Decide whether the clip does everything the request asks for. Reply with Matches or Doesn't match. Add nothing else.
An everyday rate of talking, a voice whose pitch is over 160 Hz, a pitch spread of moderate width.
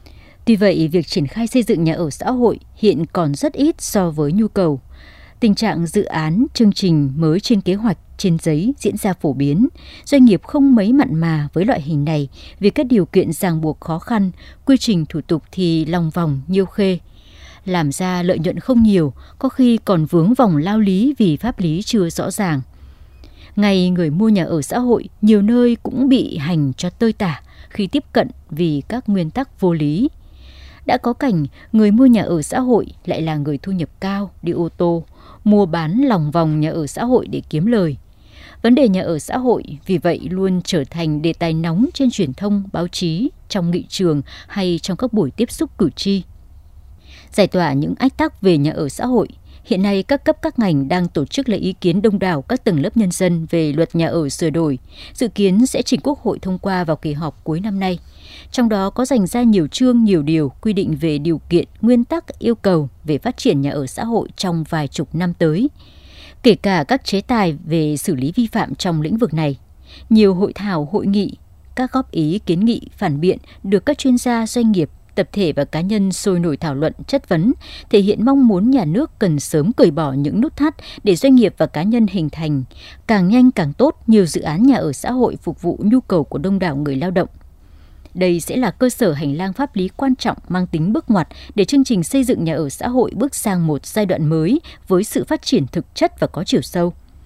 Doesn't match